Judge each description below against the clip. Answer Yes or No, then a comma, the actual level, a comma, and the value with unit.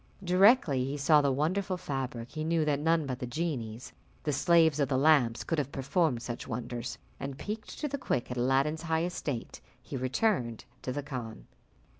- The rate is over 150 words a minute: Yes, average, 185 wpm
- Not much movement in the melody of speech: No, average, 4.5 semitones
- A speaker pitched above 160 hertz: No, medium, 140 Hz